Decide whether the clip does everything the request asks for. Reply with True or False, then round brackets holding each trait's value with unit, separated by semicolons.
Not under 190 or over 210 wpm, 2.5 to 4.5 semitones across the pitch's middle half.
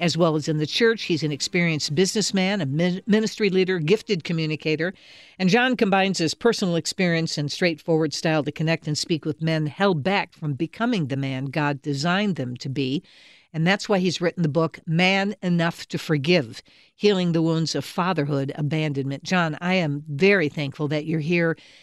False (180 wpm; 3.6 semitones)